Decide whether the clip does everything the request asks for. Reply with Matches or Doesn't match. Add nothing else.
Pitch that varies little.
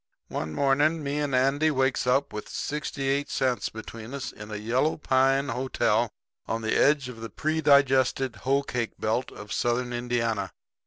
Doesn't match